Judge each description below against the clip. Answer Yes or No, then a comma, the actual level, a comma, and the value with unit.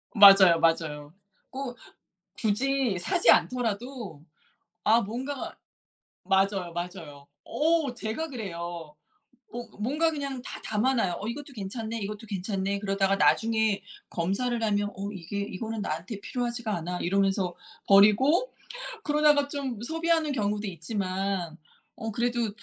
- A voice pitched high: Yes, high, 210 Hz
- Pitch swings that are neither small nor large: Yes, average, 4.5 semitones